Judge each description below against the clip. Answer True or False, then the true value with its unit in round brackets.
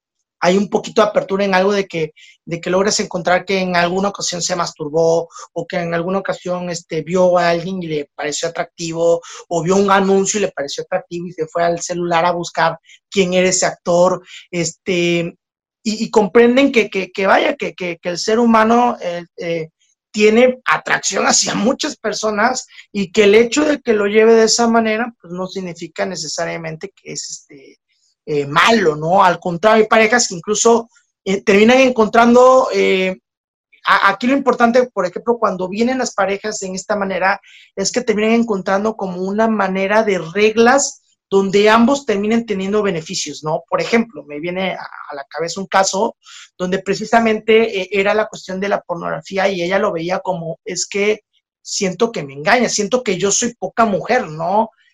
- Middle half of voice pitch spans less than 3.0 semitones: False (3.9 semitones)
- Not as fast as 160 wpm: False (185 wpm)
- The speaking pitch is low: False (195 Hz)